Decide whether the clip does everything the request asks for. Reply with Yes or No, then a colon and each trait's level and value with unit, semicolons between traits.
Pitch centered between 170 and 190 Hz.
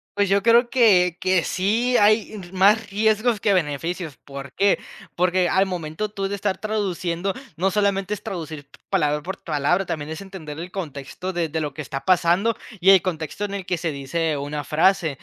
Yes: medium, 185 Hz